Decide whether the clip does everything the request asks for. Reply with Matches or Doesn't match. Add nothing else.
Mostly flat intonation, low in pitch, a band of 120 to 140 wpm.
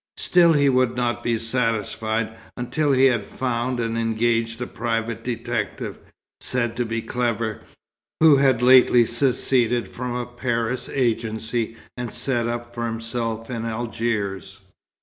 Matches